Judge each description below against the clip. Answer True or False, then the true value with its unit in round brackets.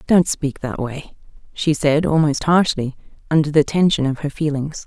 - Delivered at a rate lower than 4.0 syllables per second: False (4.7 syllables/s)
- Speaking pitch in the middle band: True (150 Hz)